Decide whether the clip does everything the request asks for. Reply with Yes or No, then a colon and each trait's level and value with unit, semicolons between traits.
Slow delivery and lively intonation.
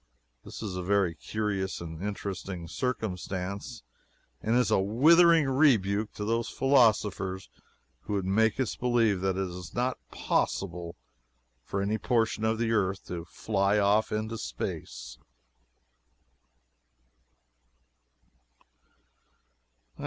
No: slow, 110 wpm; average, 3.2 semitones